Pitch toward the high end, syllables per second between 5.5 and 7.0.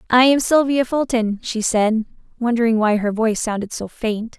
No: high, 230 Hz; 5.0 syllables/s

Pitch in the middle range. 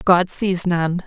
Yes: medium, 180 Hz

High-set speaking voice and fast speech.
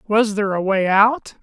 Yes: high, 210 Hz; fast, 210 wpm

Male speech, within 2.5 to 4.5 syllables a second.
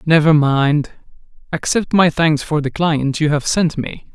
Yes: male; 4.3 syllables/s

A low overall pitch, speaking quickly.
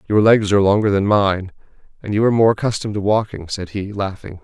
Yes: low, 100 Hz; fast, 215 wpm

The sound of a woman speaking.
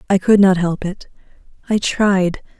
Yes: female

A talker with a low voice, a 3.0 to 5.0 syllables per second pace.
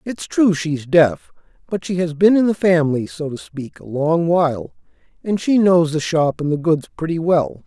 No: medium, 165 Hz; 4.7 syllables/s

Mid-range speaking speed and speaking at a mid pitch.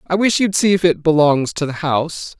No: fast, 250 wpm; medium, 160 Hz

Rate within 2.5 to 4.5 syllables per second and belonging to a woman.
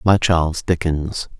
No: 4.1 syllables/s; male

